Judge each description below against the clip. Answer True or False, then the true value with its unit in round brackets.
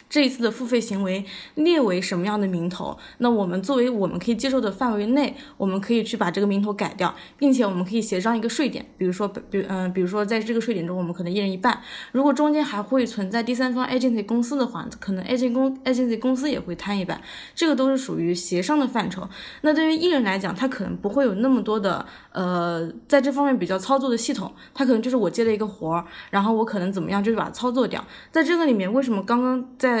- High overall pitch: True (230 Hz)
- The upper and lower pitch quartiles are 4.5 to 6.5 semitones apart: True (4.8 semitones)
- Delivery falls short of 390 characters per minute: False (395 characters per minute)